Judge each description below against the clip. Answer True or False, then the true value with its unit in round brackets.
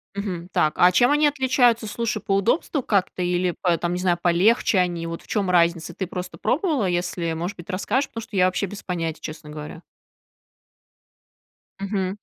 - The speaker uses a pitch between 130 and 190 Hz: True (185 Hz)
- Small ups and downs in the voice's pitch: False (3.6 semitones)